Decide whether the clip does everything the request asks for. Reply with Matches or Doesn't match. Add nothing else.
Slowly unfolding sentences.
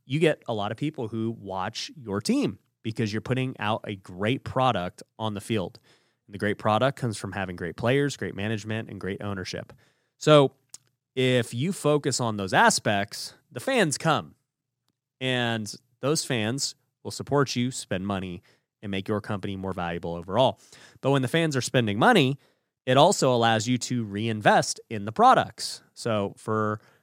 Doesn't match